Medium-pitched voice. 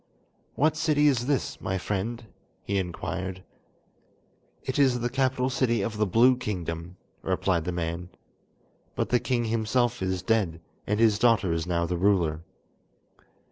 No: low, 105 Hz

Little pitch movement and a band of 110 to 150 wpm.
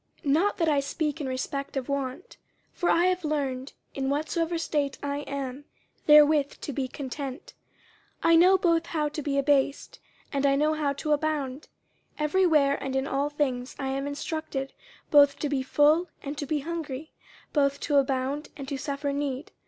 No: narrow, 2.0 semitones; average, 185 wpm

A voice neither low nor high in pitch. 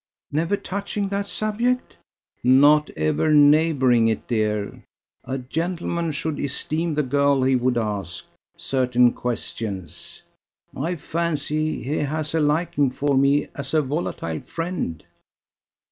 Yes: medium, 145 Hz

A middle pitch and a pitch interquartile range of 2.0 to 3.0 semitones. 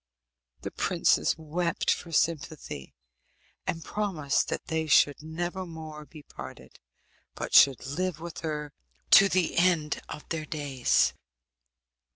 Yes: medium, 160 Hz; narrow, 2.4 semitones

